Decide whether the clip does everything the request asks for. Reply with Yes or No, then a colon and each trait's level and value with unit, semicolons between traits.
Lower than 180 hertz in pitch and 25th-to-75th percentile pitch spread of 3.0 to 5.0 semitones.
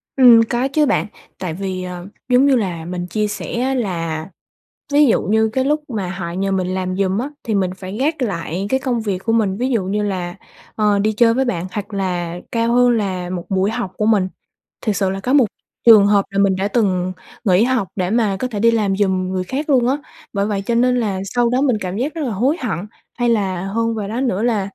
No: high, 210 Hz; average, 4.3 semitones